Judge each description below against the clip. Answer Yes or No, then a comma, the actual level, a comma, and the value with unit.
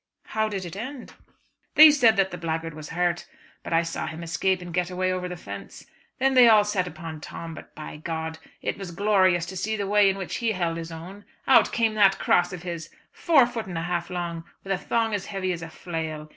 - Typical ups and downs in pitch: Yes, average, 3.7 semitones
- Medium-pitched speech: Yes, medium, 180 Hz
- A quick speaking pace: Yes, fast, 235 wpm